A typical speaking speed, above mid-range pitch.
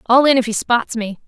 No: fast, 280 wpm; high, 235 Hz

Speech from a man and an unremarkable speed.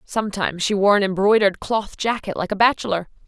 No: female; average, 185 wpm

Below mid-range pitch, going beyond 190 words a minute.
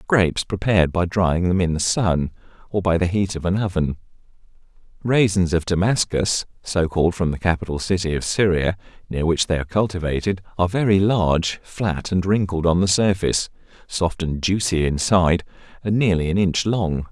No: very low, 90 Hz; average, 170 wpm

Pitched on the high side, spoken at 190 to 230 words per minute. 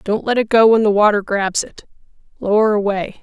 Yes: high, 210 Hz; fast, 205 wpm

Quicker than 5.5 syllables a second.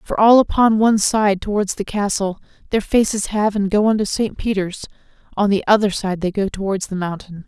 No: 5.4 syllables/s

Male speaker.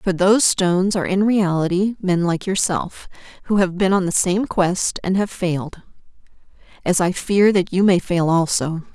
No: female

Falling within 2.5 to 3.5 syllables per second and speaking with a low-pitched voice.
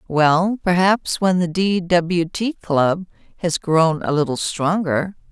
No: 3.4 syllables/s; medium, 175 Hz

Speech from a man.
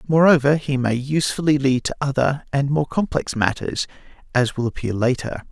Yes: male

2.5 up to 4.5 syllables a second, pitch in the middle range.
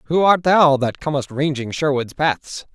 Yes: 4.4 syllables/s; medium, 145 Hz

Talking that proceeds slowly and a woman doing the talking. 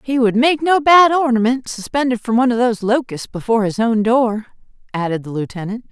No: average, 195 wpm; female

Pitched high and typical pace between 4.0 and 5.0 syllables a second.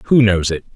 No: low, 105 Hz; 4.8 syllables/s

